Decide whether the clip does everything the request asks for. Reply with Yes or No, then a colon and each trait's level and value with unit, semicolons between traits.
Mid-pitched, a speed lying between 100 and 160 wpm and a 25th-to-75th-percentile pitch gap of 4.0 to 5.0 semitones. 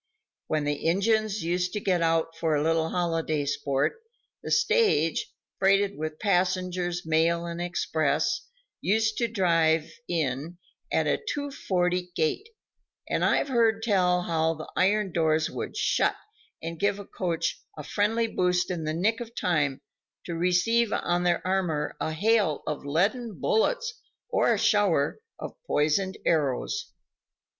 Yes: medium, 180 Hz; average, 145 wpm; average, 4.4 semitones